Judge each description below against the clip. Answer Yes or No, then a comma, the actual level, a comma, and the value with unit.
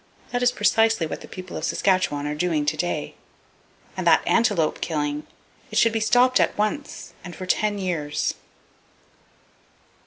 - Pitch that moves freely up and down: Yes, wide, 6.3 semitones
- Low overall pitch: No, medium, 185 Hz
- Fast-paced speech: No, average, 155 wpm